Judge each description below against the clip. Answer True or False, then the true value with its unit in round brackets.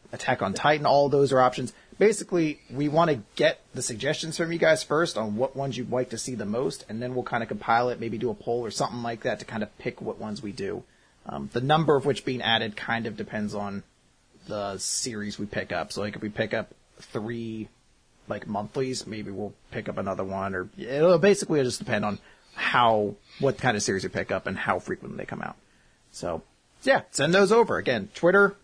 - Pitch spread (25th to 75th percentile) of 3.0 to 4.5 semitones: False (5.4 semitones)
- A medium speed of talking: False (225 wpm)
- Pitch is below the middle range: True (120 Hz)